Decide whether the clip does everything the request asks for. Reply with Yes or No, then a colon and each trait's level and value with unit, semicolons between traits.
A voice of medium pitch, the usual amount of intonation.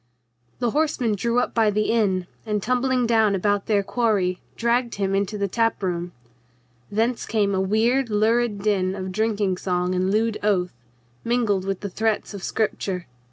No: high, 210 Hz; average, 3.1 semitones